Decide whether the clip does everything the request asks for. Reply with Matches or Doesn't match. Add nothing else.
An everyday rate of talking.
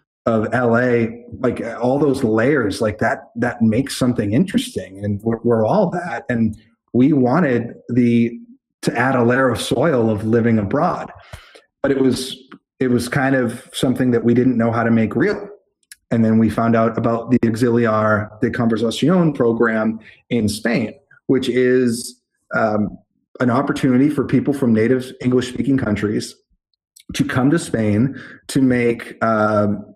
Matches